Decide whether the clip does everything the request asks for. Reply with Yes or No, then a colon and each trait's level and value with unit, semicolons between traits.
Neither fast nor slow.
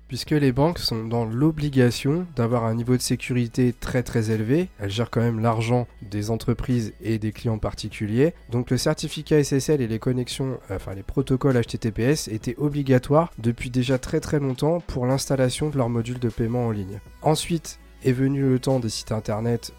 Yes: average, 180 wpm